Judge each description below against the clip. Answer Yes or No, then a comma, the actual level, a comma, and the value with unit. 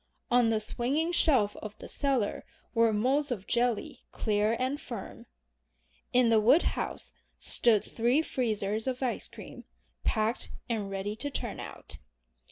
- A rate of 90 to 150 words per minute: Yes, average, 140 wpm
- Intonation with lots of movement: No, average, 3.3 semitones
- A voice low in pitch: No, high, 235 Hz